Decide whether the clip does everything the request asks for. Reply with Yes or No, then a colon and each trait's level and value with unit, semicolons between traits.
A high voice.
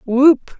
Yes: very high, 270 Hz